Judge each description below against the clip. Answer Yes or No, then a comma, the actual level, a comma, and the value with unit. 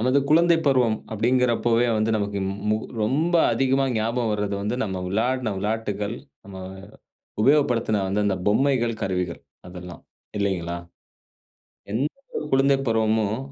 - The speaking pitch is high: No, low, 110 Hz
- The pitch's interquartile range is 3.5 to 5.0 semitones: Yes, average, 3.9 semitones